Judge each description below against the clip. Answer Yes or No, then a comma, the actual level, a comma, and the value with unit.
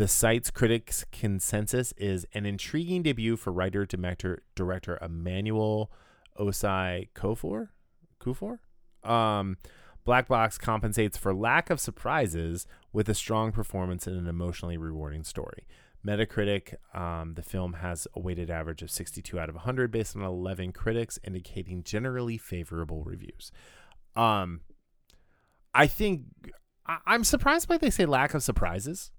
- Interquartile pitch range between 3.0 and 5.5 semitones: Yes, average, 4.5 semitones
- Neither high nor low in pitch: No, low, 100 Hz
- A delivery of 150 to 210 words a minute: No, average, 140 wpm